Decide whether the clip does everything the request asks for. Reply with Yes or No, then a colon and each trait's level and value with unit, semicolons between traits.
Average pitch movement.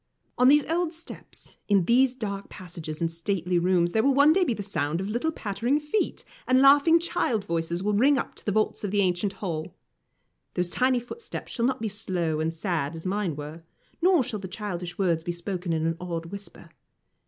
No: wide, 6.7 semitones